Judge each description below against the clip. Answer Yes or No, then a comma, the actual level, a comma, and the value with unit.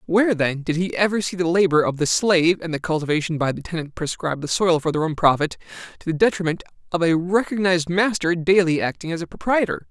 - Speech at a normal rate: No, fast, 220 wpm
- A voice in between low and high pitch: Yes, medium, 170 Hz